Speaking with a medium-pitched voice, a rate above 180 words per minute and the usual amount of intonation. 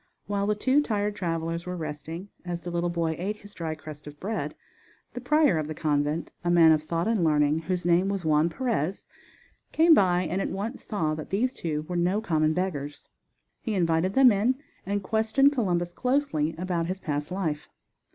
Yes: medium, 175 Hz; average, 190 wpm; average, 4.4 semitones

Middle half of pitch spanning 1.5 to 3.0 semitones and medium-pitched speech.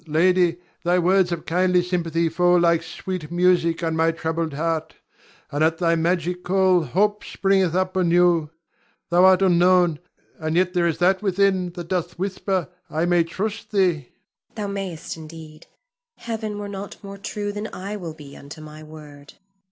Yes: narrow, 2.5 semitones; medium, 175 Hz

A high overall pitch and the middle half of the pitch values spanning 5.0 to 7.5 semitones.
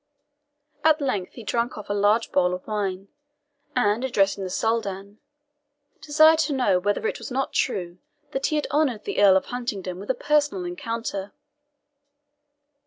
Yes: high, 210 Hz; average, 5.3 semitones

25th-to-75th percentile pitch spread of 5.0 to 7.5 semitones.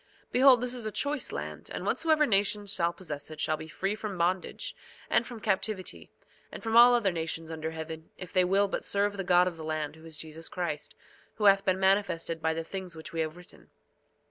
No: average, 4.1 semitones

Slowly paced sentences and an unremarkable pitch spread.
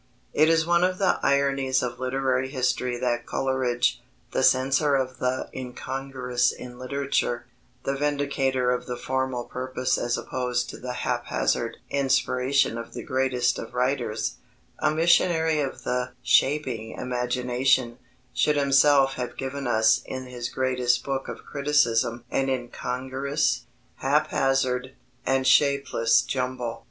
No: slow, 130 wpm; narrow, 1.7 semitones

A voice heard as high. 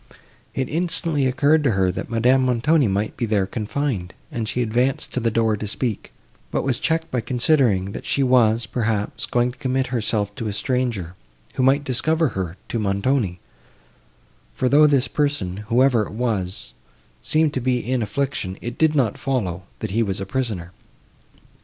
No: low, 120 Hz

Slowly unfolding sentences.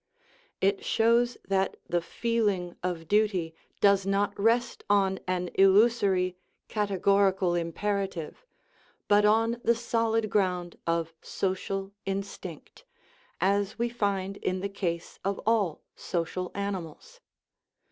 Yes: slow, 115 wpm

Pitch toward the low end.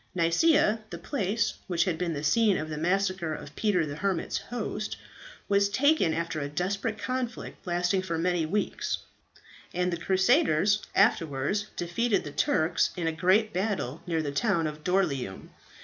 No: medium, 180 Hz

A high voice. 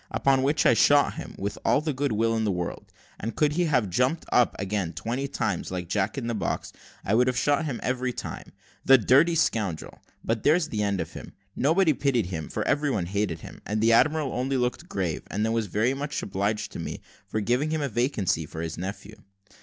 No: low, 115 Hz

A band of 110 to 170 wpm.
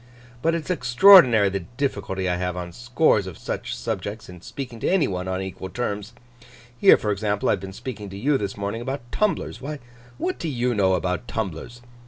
No: average, 200 wpm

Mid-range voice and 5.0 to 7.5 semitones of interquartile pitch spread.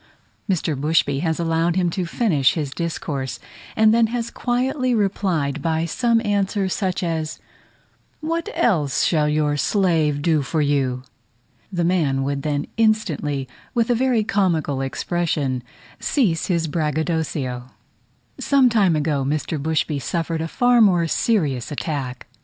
Yes: medium, 165 Hz; wide, 5.6 semitones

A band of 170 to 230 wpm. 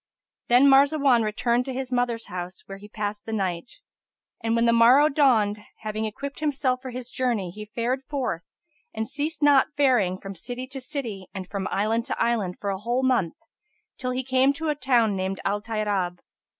Yes: average, 190 wpm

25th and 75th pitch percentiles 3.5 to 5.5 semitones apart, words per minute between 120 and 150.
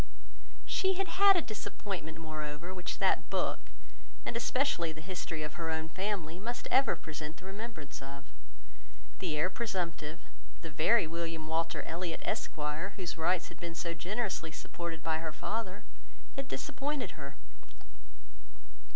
Yes: average, 4.7 semitones; average, 140 wpm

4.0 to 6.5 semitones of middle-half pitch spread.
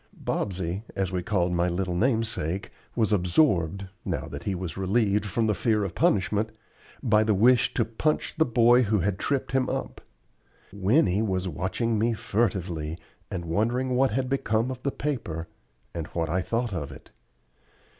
Yes: average, 4.4 semitones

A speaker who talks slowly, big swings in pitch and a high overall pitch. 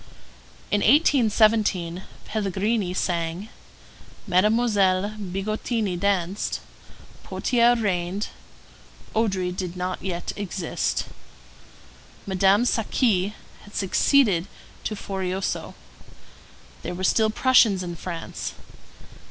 No: slow, 80 wpm; average, 3.1 semitones; high, 195 Hz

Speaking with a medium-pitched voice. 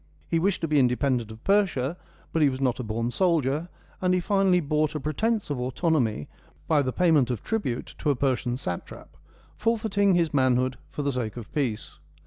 Yes: medium, 145 Hz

